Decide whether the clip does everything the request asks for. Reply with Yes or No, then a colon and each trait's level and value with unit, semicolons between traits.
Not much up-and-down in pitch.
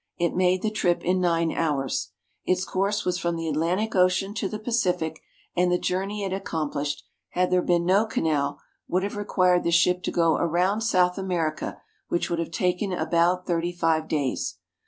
Yes: narrow, 2.1 semitones